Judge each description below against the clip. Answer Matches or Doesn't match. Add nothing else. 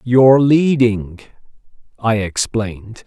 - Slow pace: Matches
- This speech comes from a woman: Doesn't match